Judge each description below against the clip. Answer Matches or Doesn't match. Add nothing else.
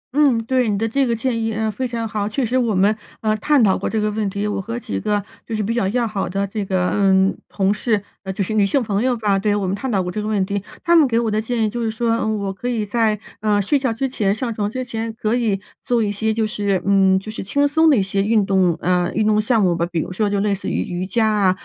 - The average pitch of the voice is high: Matches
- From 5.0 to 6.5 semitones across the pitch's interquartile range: Doesn't match